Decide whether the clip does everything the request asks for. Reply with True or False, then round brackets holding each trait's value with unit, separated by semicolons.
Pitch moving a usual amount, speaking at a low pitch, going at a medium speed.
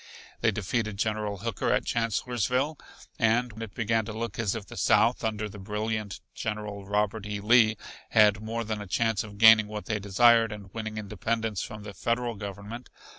False (1.7 semitones; 110 Hz; 180 wpm)